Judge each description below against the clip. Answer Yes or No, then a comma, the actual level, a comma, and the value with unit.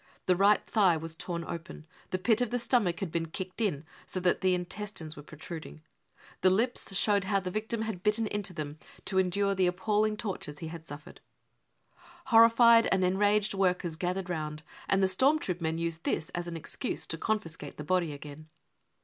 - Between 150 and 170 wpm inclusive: No, average, 195 wpm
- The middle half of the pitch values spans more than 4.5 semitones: No, average, 4.2 semitones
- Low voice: No, medium, 185 Hz